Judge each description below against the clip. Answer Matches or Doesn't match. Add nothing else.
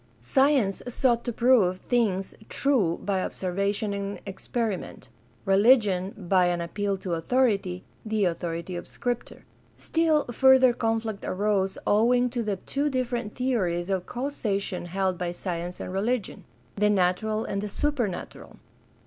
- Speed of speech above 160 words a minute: Doesn't match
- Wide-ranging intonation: Doesn't match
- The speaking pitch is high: Matches